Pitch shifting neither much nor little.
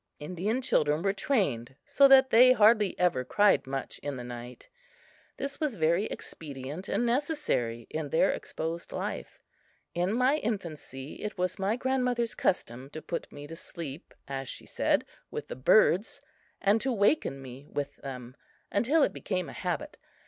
No: wide, 9.0 semitones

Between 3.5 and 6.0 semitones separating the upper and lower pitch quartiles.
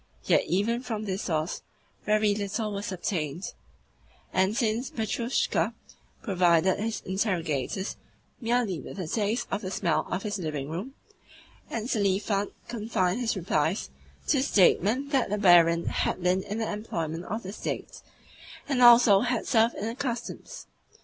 Yes: average, 4.0 semitones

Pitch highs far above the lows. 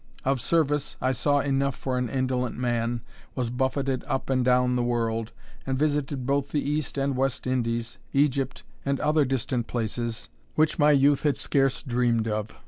No: narrow, 2.4 semitones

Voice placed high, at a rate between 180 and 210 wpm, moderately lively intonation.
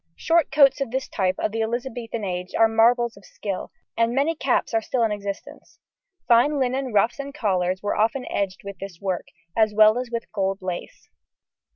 Yes: high, 225 Hz; average, 190 wpm; average, 3.9 semitones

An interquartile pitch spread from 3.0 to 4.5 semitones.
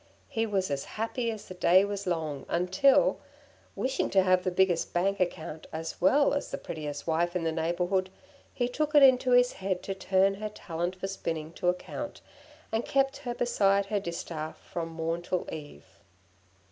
Yes: average, 4.2 semitones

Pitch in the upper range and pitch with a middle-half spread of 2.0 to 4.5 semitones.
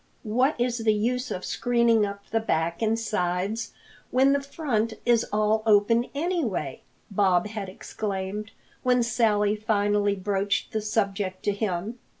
Yes: high, 215 Hz; average, 2.7 semitones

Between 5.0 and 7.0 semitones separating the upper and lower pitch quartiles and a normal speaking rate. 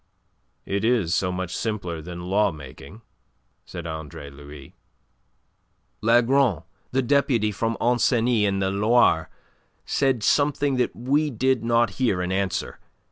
No: wide, 5.4 semitones; slow, 130 wpm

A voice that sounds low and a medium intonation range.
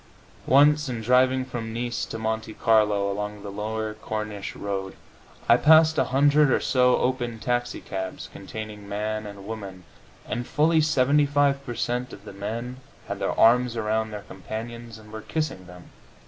Yes: low, 115 Hz; average, 3.4 semitones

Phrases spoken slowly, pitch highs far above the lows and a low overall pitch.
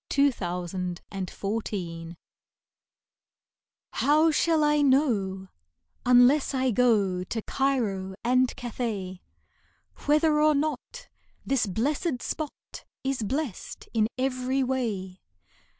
No: slow, 105 wpm; wide, 6.5 semitones; very high, 250 Hz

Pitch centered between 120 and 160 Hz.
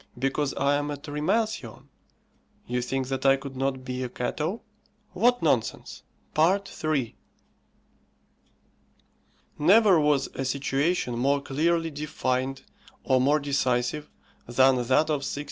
Yes: medium, 140 Hz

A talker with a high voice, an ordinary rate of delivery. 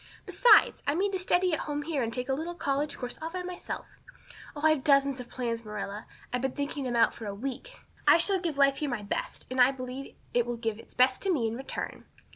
No: very high, 275 Hz; fast, 245 wpm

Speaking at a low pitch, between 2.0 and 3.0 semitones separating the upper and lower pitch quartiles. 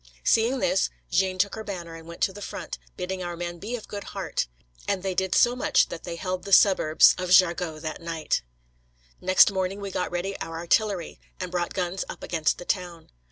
No: medium, 185 Hz; narrow, 2.4 semitones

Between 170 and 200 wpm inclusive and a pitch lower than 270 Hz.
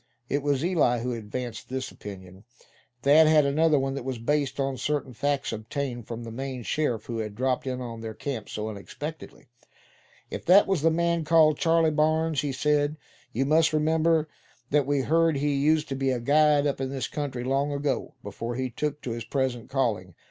Yes: average, 195 wpm; medium, 140 Hz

